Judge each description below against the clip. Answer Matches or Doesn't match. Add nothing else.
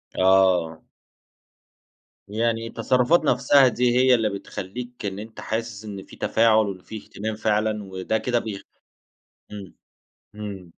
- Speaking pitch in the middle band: Doesn't match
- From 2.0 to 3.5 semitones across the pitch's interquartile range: Matches